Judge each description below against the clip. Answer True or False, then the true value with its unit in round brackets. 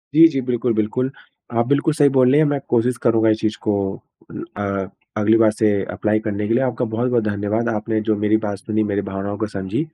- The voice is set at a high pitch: False (110 Hz)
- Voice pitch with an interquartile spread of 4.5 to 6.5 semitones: False (3.1 semitones)